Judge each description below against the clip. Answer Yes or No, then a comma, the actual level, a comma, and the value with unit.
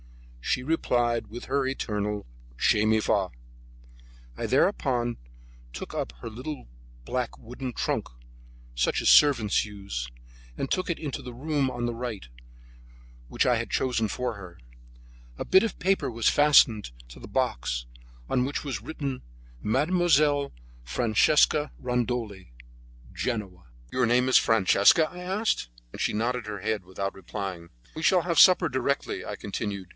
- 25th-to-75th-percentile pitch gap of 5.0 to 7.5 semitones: Yes, average, 5.3 semitones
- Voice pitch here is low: Yes, low, 120 Hz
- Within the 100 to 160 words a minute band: Yes, average, 145 wpm